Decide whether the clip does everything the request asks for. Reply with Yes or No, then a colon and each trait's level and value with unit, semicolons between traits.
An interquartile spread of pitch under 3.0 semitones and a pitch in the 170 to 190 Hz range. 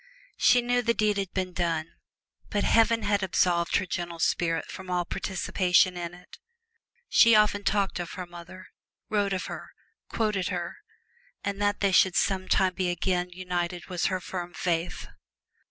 Yes: narrow, 2.4 semitones; medium, 185 Hz